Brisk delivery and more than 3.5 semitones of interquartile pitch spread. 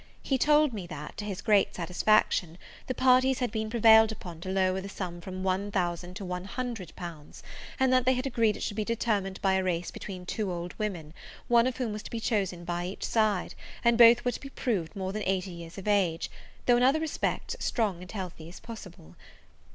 Yes: fast, 220 wpm; average, 4.4 semitones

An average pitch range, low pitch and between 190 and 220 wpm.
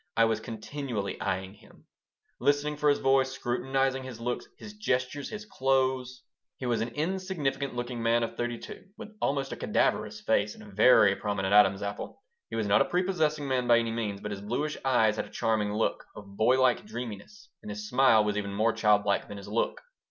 Yes: average, 4.5 semitones; low, 120 Hz; fast, 205 wpm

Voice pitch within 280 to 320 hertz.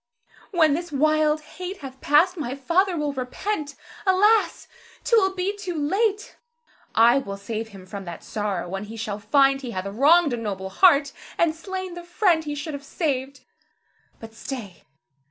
Yes: very high, 290 Hz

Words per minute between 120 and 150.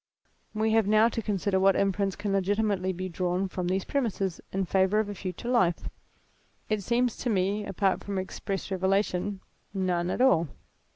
No: average, 170 wpm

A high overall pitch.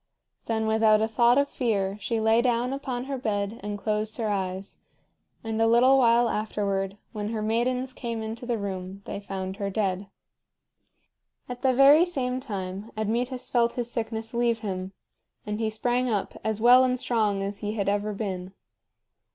Yes: high, 220 Hz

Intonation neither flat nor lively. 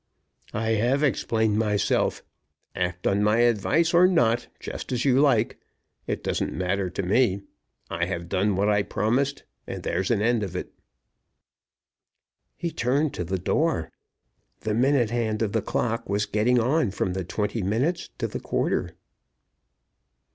Yes: average, 4.0 semitones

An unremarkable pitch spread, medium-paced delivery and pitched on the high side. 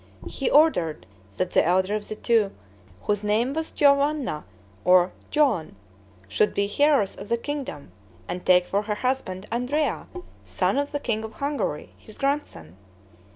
No: wide, 7.4 semitones; average, 155 wpm; high, 220 Hz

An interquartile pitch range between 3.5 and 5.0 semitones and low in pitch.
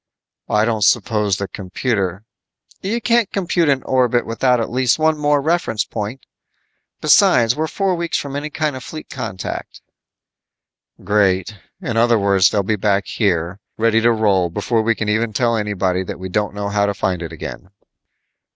Yes: average, 4.7 semitones; low, 110 Hz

